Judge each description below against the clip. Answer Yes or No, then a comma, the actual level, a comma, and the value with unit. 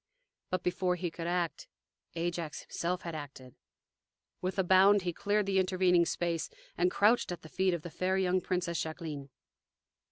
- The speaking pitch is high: No, medium, 180 Hz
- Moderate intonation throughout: No, narrow, 1.8 semitones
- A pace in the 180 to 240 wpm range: No, average, 165 wpm